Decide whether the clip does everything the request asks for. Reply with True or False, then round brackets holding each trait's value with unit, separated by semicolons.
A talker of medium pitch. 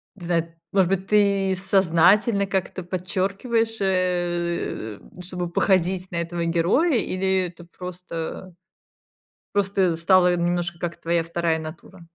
True (180 Hz)